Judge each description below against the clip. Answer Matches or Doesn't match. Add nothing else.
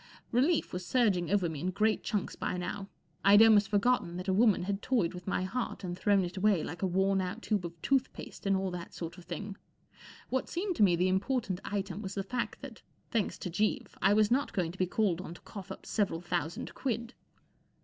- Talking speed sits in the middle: Doesn't match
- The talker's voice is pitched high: Matches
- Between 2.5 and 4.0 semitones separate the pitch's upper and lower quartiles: Matches